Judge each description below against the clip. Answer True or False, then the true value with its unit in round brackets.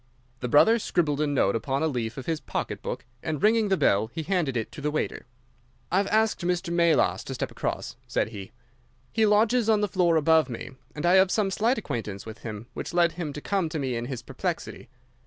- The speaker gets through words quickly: True (225 wpm)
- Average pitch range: False (6.6 semitones)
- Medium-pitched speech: True (160 Hz)